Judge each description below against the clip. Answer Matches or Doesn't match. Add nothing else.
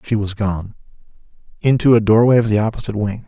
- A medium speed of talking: Matches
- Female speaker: Doesn't match